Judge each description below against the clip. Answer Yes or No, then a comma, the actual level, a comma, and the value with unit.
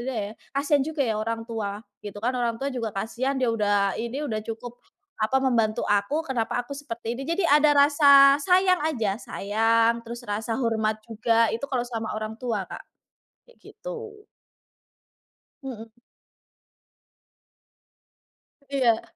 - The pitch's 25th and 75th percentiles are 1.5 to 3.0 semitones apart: No, average, 4.0 semitones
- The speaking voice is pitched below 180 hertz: No, high, 235 Hz